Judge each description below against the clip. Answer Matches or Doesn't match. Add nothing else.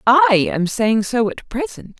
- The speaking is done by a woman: Matches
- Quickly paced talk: Doesn't match